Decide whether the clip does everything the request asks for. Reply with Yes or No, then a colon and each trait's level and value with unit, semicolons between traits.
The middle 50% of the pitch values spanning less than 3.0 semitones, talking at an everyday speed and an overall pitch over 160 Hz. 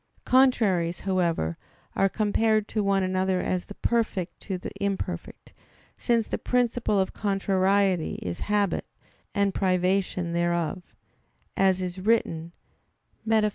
No: narrow, 2.5 semitones; slow, 120 wpm; high, 190 Hz